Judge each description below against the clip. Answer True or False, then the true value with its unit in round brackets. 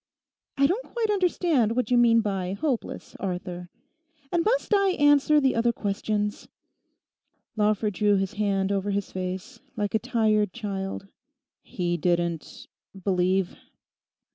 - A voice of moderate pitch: False (210 Hz)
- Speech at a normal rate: False (125 wpm)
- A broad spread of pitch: False (4.8 semitones)